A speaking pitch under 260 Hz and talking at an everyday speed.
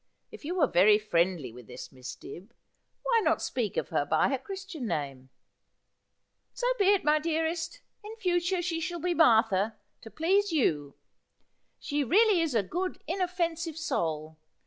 No: very high, 310 Hz; average, 170 wpm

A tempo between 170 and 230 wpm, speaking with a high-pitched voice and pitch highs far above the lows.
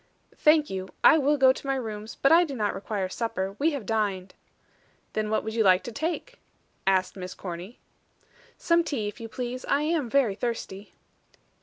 Yes: average, 185 wpm; high, 225 Hz; wide, 6.0 semitones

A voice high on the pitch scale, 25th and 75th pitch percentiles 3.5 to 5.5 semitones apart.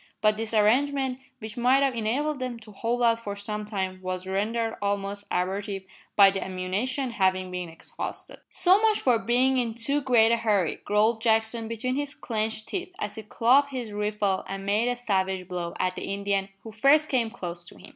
Yes: high, 220 Hz; average, 3.9 semitones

